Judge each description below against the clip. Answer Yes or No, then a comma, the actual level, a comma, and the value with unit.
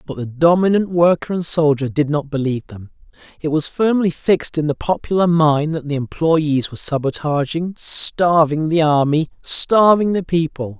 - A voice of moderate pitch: Yes, medium, 155 Hz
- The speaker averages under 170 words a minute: Yes, average, 160 wpm